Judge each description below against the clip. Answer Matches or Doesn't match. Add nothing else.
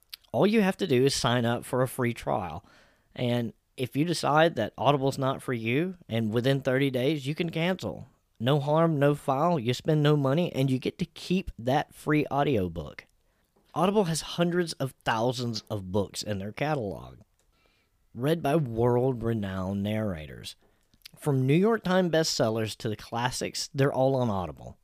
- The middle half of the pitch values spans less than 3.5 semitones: Doesn't match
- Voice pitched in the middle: Doesn't match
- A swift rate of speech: Doesn't match